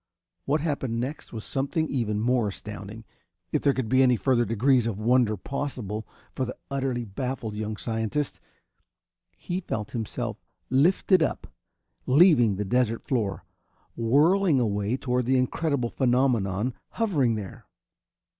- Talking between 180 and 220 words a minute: No, slow, 135 wpm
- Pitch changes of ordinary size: Yes, average, 3.9 semitones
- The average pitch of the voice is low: Yes, low, 125 Hz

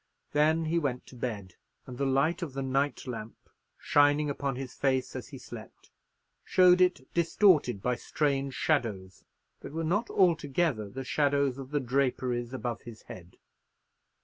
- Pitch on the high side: No, low, 135 Hz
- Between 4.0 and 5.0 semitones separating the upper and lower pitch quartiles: No, average, 3.6 semitones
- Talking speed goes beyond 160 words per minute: No, average, 155 wpm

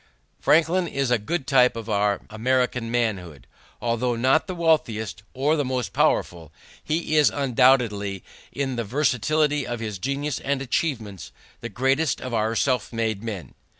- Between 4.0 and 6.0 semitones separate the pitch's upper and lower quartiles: Yes, average, 4.3 semitones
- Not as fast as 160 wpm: Yes, average, 150 wpm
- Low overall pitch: Yes, low, 125 Hz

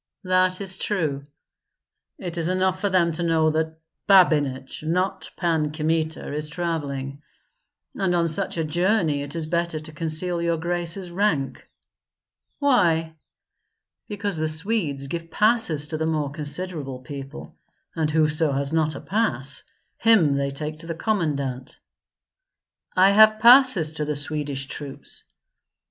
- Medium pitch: Yes, medium, 160 Hz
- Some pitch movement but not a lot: Yes, average, 3.6 semitones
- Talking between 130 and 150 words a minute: Yes, average, 140 wpm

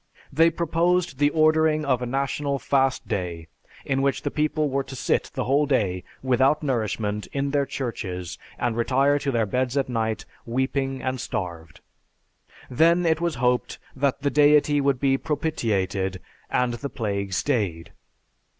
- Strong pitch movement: No, average, 4.3 semitones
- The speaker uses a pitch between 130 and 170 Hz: Yes, low, 135 Hz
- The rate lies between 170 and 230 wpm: No, average, 155 wpm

